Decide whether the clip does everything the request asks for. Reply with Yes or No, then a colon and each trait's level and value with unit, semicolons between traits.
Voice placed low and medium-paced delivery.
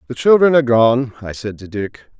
No: low, 120 Hz; fast, 220 wpm